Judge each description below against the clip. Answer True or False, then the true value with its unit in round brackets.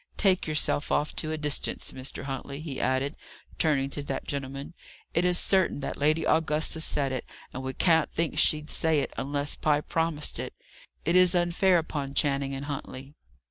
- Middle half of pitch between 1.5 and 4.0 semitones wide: True (2.9 semitones)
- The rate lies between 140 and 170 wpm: False (180 wpm)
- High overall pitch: False (150 Hz)